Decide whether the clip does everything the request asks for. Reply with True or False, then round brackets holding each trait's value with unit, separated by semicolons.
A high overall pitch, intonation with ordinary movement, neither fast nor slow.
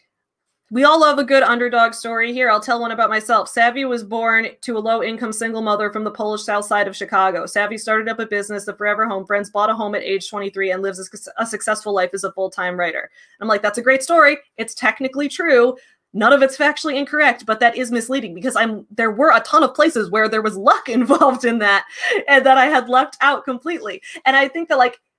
False (230 Hz; 4.2 semitones; 230 wpm)